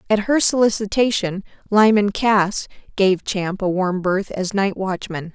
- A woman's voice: Yes, female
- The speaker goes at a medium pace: Yes, average, 145 wpm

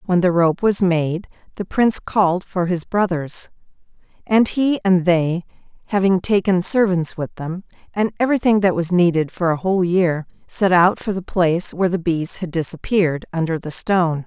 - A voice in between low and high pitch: Yes, medium, 180 Hz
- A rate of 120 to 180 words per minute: Yes, average, 175 wpm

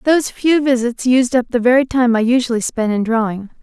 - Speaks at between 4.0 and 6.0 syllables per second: Yes, 5.6 syllables/s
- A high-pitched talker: Yes, high, 245 Hz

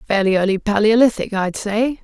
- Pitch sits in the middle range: No, high, 210 Hz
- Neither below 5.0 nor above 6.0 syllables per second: Yes, 5.2 syllables/s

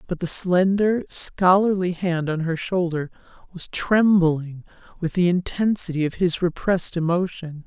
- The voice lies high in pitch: No, medium, 175 Hz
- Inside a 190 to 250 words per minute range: No, slow, 135 wpm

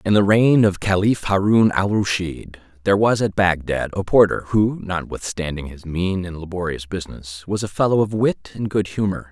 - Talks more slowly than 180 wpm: No, average, 185 wpm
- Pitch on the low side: Yes, very low, 95 Hz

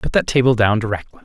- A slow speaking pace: No, fast, 240 wpm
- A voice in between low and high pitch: No, low, 115 Hz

